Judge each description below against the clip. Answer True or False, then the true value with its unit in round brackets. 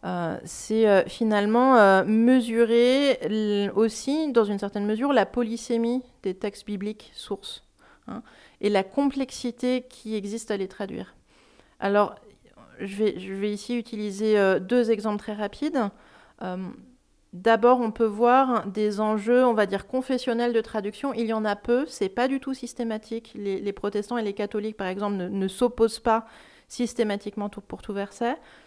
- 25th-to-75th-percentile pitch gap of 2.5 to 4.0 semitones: True (2.9 semitones)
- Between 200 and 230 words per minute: False (150 wpm)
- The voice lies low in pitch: False (220 Hz)